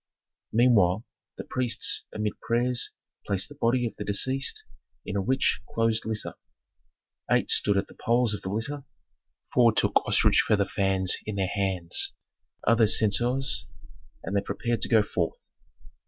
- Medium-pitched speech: No, low, 110 Hz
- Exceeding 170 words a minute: No, average, 150 wpm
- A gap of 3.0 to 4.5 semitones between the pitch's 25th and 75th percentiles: Yes, average, 3.3 semitones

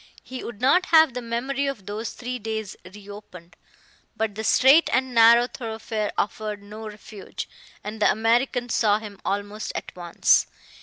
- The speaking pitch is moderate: No, high, 220 Hz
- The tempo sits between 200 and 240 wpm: No, average, 160 wpm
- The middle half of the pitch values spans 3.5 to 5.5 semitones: No, average, 3.1 semitones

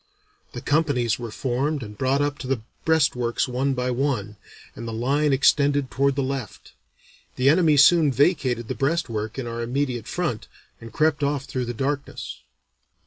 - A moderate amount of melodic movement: Yes, average, 3.1 semitones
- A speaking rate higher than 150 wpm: Yes, average, 165 wpm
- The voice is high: No, low, 135 Hz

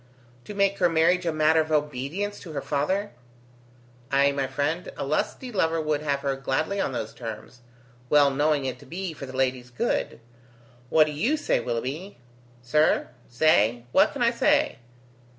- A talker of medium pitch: Yes, medium, 150 Hz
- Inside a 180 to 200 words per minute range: No, average, 170 wpm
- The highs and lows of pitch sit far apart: No, average, 3.9 semitones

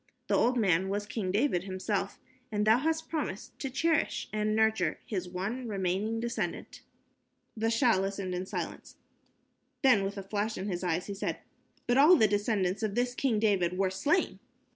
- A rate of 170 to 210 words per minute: Yes, average, 175 wpm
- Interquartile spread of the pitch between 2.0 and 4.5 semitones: Yes, average, 3.7 semitones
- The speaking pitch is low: No, high, 210 Hz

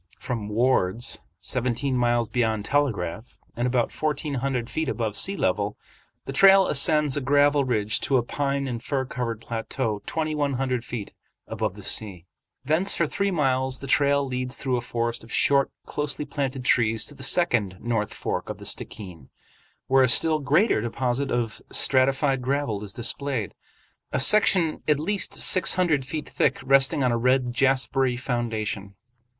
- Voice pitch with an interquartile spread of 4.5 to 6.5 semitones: No, average, 3.4 semitones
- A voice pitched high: No, low, 130 Hz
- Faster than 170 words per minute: No, average, 165 wpm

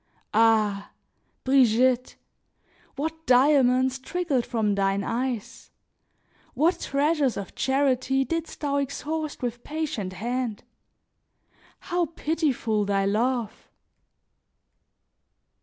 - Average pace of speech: No, slow, 85 wpm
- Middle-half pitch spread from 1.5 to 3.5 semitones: No, average, 4.4 semitones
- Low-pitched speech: No, very high, 255 Hz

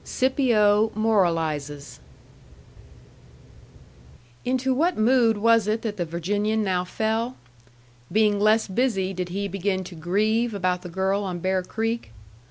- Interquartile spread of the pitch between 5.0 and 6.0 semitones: No, average, 3.5 semitones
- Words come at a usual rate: No, slow, 130 wpm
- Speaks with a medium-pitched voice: No, high, 205 Hz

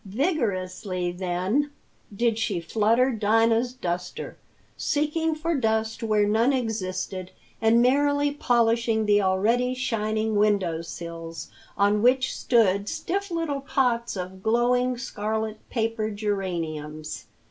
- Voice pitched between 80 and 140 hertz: No, high, 220 Hz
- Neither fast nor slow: No, slow, 110 wpm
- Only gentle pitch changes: No, average, 4.5 semitones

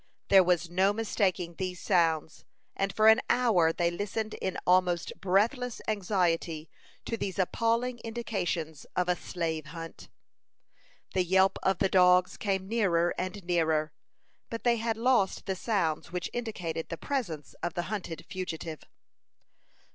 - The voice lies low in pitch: No, medium, 185 Hz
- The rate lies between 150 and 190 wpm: No, average, 140 wpm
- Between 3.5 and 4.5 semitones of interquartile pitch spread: Yes, average, 4.0 semitones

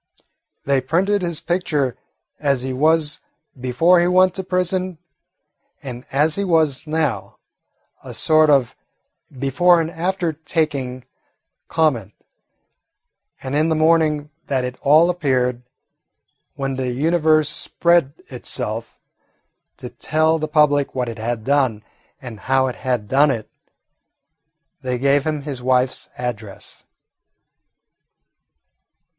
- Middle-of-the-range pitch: Yes, medium, 145 Hz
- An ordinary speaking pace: No, slow, 120 wpm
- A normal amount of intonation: Yes, average, 4.1 semitones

